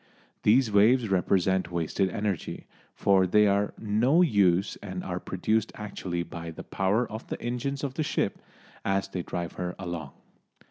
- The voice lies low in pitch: Yes, low, 100 Hz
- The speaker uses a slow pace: No, average, 155 wpm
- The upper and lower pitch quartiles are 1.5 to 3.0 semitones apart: No, average, 3.5 semitones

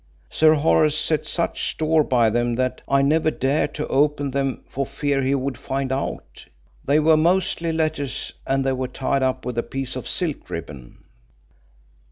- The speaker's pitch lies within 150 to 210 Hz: No, medium, 140 Hz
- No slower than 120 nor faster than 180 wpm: Yes, average, 175 wpm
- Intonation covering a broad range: No, average, 3.0 semitones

